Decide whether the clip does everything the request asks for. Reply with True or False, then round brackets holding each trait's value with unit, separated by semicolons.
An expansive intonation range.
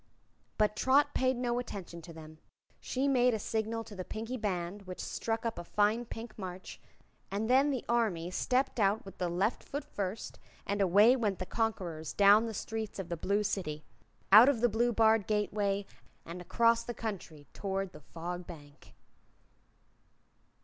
False (4.0 semitones)